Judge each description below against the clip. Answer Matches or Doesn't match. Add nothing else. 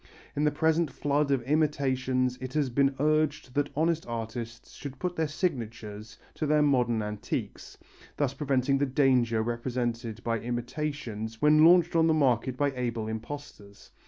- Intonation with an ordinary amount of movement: Matches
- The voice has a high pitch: Doesn't match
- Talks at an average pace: Matches